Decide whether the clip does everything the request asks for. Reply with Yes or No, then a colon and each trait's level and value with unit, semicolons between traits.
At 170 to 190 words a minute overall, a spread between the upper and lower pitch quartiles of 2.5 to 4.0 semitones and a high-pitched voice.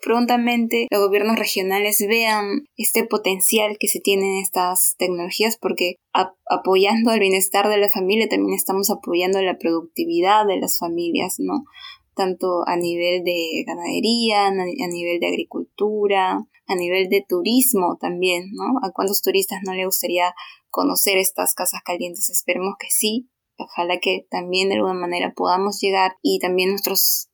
No: average, 150 wpm; average, 2.8 semitones; high, 195 Hz